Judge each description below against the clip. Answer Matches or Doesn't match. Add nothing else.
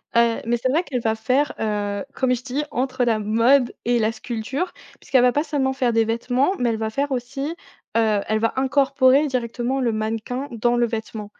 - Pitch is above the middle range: Matches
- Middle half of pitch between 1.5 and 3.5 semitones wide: Matches